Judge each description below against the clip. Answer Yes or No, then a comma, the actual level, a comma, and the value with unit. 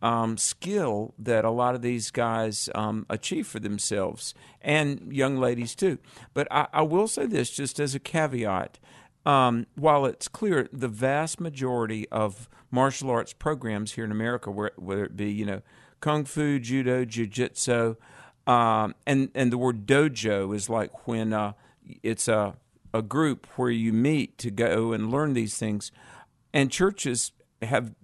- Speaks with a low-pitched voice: Yes, low, 120 Hz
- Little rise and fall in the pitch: No, average, 3.8 semitones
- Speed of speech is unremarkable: Yes, average, 165 wpm